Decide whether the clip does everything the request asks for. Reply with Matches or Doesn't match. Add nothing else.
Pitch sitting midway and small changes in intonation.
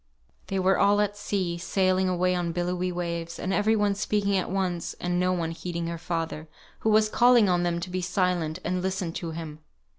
Matches